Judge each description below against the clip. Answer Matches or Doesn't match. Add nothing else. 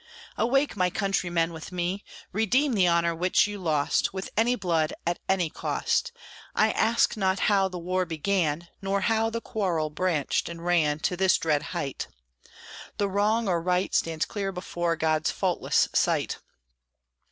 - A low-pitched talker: Doesn't match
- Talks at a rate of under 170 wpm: Matches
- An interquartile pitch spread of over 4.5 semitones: Doesn't match